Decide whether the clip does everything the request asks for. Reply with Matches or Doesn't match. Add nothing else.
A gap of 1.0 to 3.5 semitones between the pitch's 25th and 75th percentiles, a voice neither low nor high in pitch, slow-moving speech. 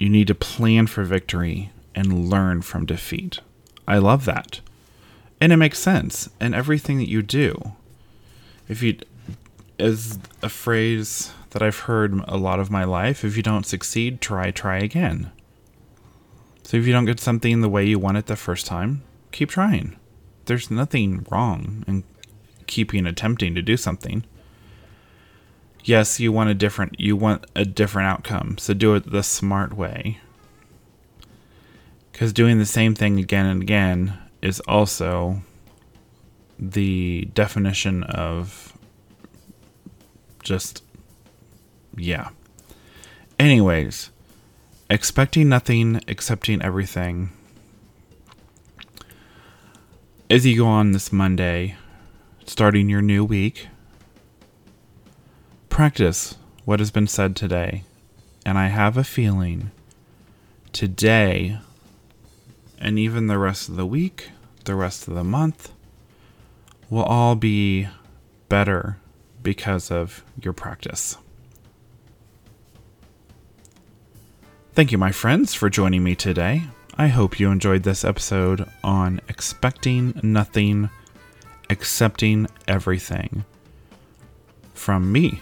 Doesn't match